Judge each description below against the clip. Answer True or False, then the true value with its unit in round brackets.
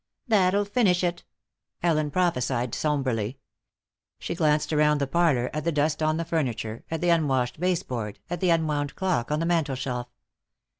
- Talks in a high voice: False (155 Hz)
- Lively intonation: False (4.5 semitones)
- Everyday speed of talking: True (160 wpm)